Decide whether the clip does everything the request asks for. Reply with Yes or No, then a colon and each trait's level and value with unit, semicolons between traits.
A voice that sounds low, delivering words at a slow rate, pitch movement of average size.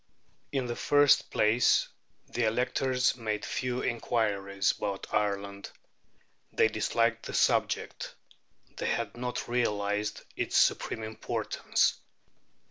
Yes: low, 110 Hz; slow, 105 wpm; average, 3.1 semitones